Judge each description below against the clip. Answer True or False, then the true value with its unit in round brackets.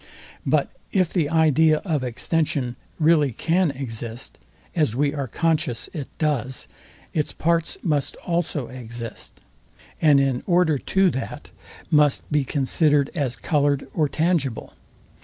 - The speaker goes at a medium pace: False (125 wpm)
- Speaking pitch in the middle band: True (150 Hz)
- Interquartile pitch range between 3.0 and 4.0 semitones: True (3.6 semitones)